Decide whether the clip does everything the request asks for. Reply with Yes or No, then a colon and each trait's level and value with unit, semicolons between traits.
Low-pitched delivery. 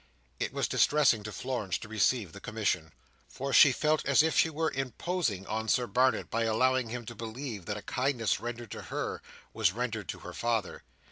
Yes: low, 120 Hz